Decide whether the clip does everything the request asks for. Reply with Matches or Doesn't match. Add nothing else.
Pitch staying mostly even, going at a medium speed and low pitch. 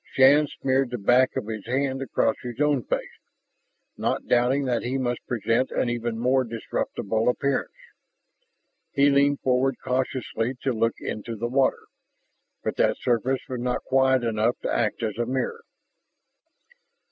Matches